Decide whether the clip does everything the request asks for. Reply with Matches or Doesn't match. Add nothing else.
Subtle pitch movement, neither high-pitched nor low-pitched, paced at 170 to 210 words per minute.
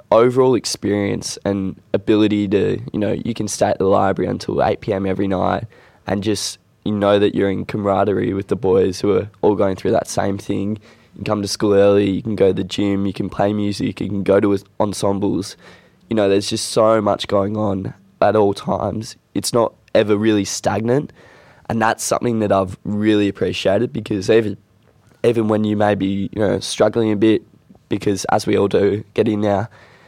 Doesn't match